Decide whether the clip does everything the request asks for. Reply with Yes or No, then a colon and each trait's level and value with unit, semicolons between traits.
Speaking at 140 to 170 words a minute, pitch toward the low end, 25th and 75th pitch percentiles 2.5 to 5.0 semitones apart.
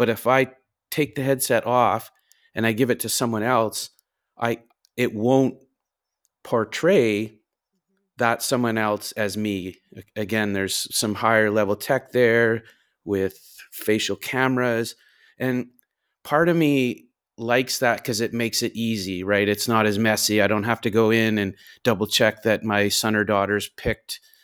Yes: average, 155 wpm; low, 115 Hz; average, 2.8 semitones